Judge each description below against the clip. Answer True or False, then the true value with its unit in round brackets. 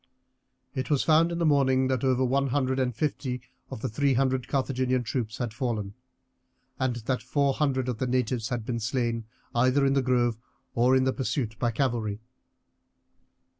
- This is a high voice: False (130 Hz)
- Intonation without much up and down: True (2.1 semitones)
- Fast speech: False (175 wpm)